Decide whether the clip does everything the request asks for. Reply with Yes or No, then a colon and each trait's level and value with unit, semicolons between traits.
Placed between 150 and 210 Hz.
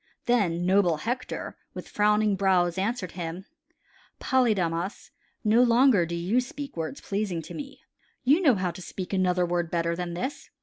Yes: high, 190 Hz